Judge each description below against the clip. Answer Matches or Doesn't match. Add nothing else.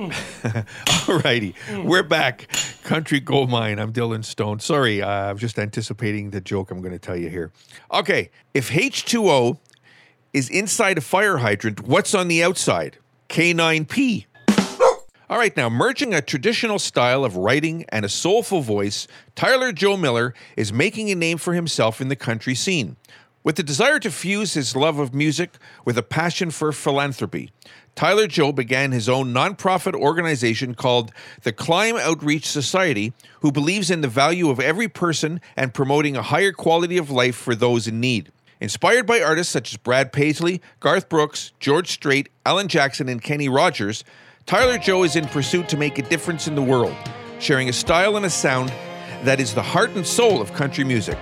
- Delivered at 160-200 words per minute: Matches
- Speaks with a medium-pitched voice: Matches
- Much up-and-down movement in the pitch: Matches